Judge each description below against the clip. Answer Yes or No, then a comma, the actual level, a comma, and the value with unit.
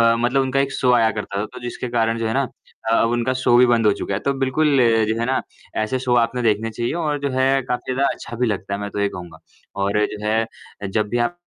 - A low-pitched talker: Yes, low, 120 Hz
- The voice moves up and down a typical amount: Yes, average, 3.2 semitones